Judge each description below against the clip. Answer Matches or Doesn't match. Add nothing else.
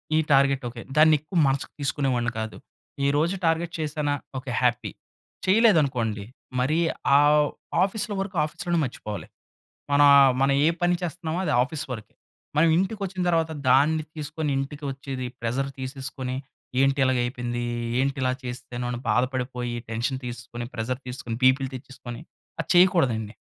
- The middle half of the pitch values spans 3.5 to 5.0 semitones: Matches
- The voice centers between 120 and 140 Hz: Matches